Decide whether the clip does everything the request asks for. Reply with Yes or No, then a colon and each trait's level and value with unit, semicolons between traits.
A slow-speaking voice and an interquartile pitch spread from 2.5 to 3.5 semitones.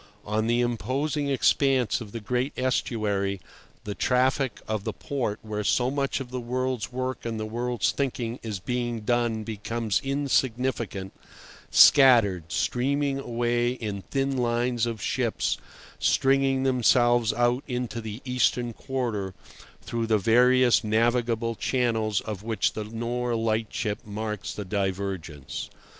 Yes: slow, 130 wpm; average, 2.8 semitones